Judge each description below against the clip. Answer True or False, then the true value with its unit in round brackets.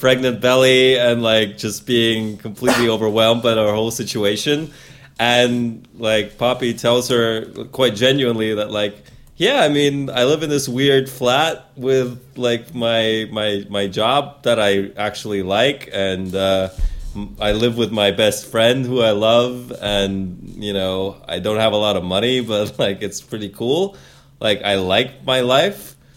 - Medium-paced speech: True (165 wpm)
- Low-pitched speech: True (115 Hz)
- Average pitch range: True (3.4 semitones)